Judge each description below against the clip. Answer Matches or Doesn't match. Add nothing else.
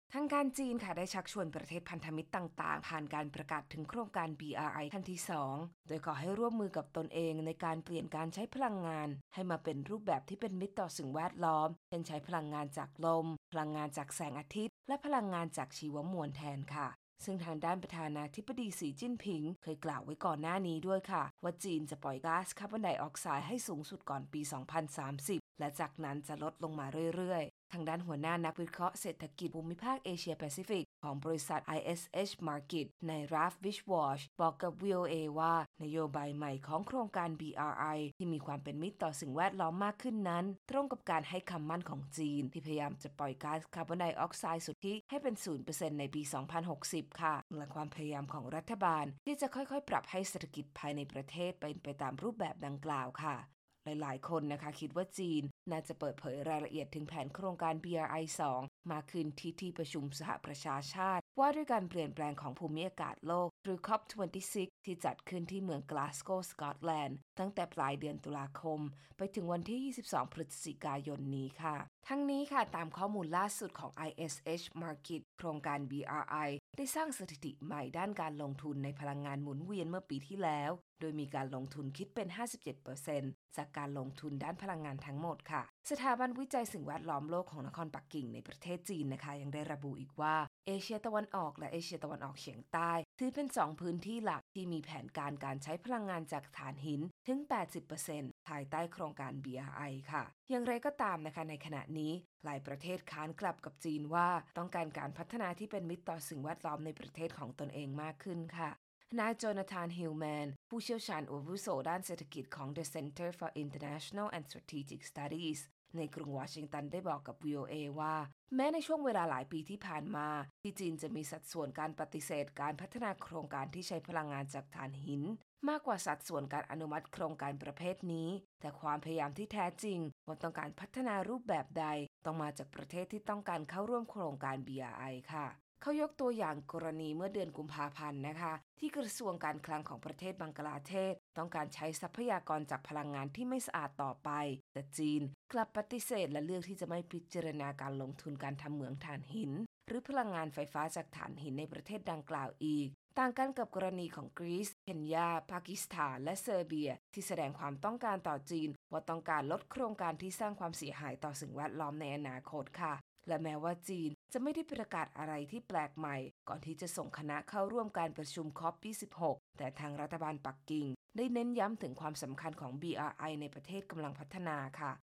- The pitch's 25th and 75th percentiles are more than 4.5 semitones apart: Doesn't match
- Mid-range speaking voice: Matches